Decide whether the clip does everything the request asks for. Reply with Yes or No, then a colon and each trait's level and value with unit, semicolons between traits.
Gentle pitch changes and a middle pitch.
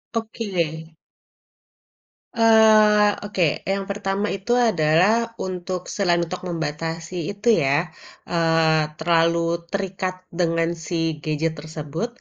No: average, 3.6 semitones; medium, 175 Hz